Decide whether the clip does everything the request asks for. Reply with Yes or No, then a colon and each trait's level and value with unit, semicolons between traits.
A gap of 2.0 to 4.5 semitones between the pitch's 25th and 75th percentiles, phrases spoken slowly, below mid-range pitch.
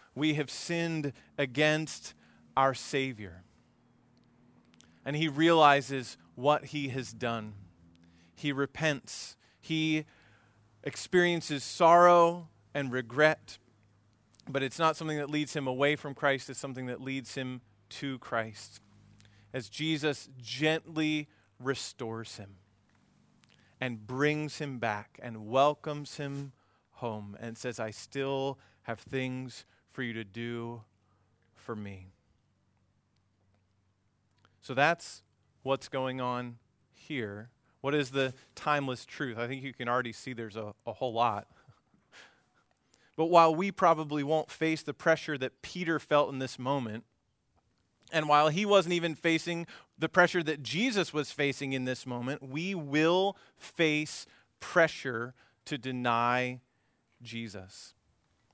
No: wide, 5.4 semitones; slow, 125 wpm; low, 130 Hz